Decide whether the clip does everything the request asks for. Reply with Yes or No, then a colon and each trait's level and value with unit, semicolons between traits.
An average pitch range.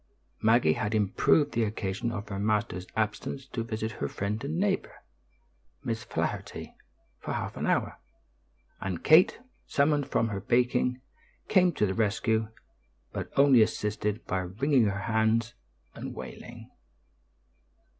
Yes: average, 3.5 semitones